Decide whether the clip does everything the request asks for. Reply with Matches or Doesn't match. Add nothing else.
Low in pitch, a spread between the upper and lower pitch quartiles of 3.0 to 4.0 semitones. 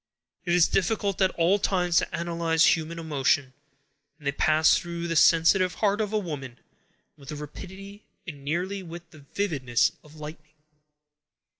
Doesn't match